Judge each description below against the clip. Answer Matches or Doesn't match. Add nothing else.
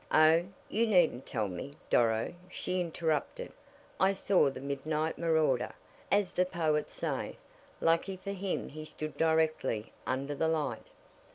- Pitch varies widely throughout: Doesn't match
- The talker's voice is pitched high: Doesn't match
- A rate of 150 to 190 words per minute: Doesn't match